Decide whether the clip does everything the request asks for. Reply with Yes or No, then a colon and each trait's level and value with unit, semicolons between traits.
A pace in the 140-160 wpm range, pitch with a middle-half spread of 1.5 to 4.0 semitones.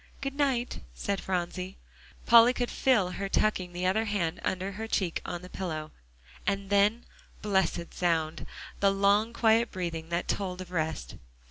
Yes: average, 155 wpm; average, 3.3 semitones